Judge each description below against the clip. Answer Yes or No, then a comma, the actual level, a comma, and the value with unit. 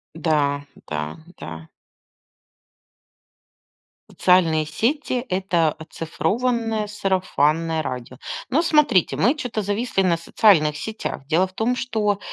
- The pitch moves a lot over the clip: Yes, wide, 6.2 semitones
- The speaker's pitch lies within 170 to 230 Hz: Yes, medium, 185 Hz